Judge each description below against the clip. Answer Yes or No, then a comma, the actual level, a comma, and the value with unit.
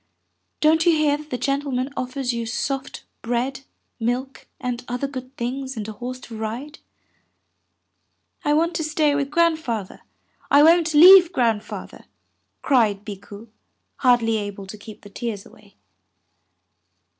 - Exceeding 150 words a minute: No, average, 140 wpm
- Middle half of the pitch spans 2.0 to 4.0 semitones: No, average, 4.5 semitones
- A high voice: Yes, very high, 255 Hz